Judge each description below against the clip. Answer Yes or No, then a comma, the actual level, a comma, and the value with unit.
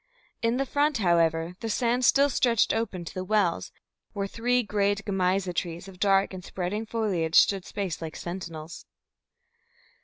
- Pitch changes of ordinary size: Yes, average, 4.3 semitones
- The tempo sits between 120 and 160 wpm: Yes, average, 155 wpm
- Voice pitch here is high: Yes, high, 195 Hz